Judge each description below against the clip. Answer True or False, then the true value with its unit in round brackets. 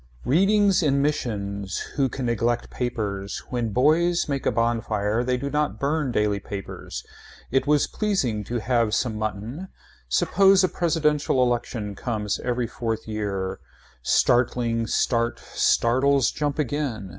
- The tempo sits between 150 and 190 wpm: False (135 wpm)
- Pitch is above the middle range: False (120 Hz)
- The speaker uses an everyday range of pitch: True (5.0 semitones)